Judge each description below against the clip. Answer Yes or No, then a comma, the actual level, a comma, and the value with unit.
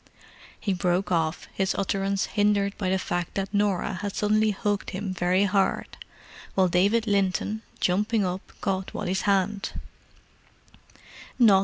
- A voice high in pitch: Yes, high, 195 Hz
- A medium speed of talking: No, slow, 130 wpm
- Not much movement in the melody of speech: Yes, narrow, 1.8 semitones